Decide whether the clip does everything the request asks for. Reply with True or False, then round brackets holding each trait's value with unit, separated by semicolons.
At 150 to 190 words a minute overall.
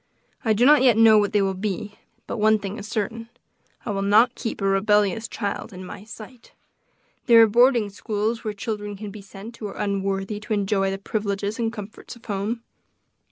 False (200 wpm)